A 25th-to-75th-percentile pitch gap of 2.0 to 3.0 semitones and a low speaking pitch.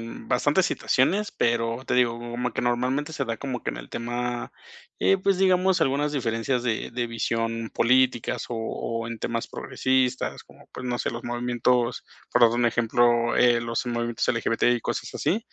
No: narrow, 1.6 semitones; low, 120 Hz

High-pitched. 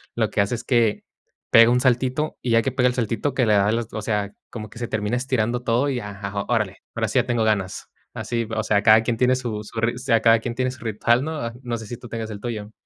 No: low, 115 Hz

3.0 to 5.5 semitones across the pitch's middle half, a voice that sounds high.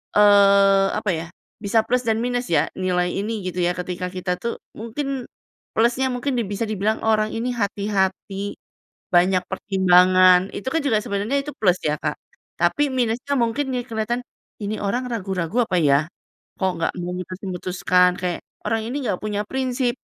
Yes: average, 4.4 semitones; high, 205 Hz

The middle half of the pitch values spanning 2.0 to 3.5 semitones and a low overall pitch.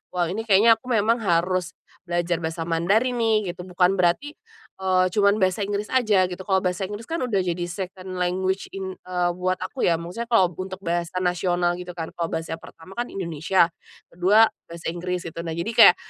No: average, 2.8 semitones; medium, 185 Hz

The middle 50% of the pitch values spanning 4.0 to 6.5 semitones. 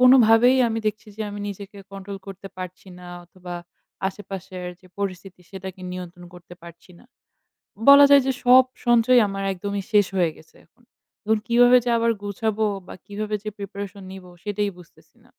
No: average, 3.2 semitones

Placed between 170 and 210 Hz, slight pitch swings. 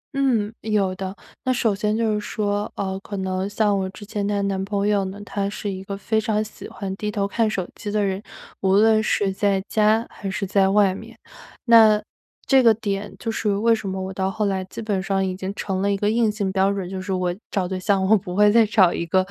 Yes: high, 200 Hz; narrow, 1.8 semitones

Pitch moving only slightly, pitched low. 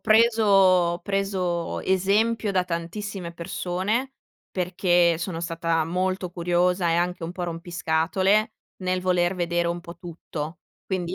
No: narrow, 1.9 semitones; medium, 180 Hz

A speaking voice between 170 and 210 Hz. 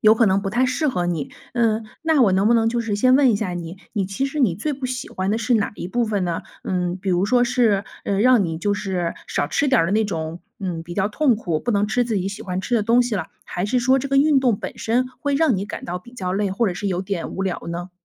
Yes: high, 205 Hz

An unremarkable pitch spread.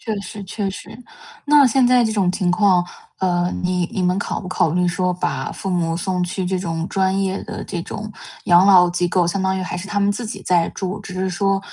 No: narrow, 2.1 semitones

